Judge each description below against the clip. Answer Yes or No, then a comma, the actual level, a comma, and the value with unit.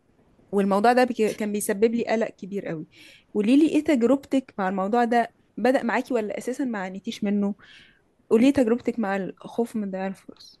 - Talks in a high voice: Yes, high, 230 Hz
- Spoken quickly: Yes, fast, 170 wpm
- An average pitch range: Yes, average, 3.4 semitones